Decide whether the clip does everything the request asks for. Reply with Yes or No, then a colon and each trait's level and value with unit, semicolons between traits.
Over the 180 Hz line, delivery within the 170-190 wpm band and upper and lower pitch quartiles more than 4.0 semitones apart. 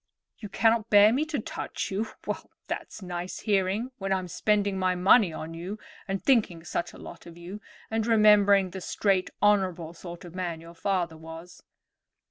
No: high, 190 Hz; average, 175 wpm; average, 3.2 semitones